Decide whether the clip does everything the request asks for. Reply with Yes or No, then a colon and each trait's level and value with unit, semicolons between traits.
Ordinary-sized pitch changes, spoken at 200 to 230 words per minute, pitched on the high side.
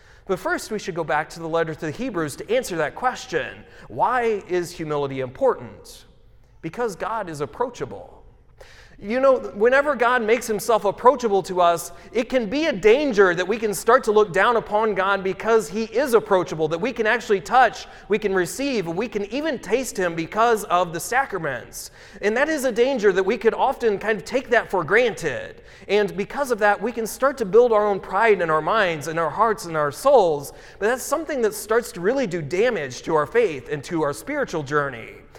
No: wide, 5.7 semitones; fast, 205 wpm; high, 215 Hz